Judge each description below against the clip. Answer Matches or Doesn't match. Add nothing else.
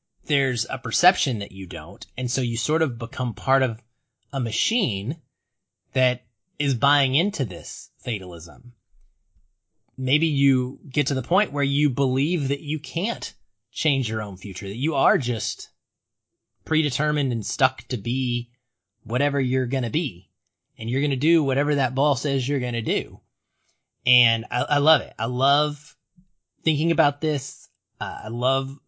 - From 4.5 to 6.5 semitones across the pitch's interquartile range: Doesn't match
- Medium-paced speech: Matches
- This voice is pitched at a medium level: Doesn't match